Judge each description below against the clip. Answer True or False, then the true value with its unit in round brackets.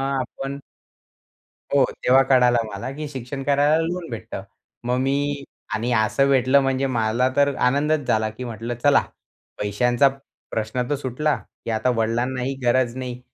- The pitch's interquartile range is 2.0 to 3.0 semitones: True (2.7 semitones)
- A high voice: False (130 Hz)